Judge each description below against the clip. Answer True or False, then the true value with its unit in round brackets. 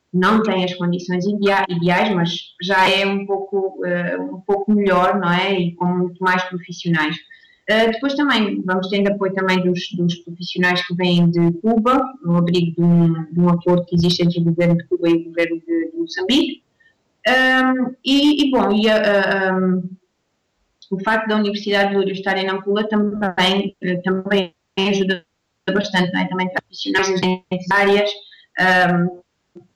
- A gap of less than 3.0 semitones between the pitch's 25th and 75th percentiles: True (2.5 semitones)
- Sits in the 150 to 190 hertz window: True (185 Hz)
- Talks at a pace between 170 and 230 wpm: True (175 wpm)